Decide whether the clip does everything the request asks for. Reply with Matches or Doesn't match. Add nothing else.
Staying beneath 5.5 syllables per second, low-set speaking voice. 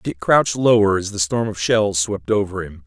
Matches